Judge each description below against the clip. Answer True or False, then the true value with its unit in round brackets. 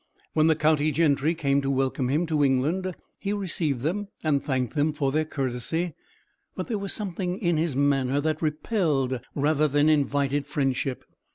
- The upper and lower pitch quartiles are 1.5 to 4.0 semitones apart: True (2.9 semitones)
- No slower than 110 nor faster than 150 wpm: False (170 wpm)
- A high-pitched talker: False (150 Hz)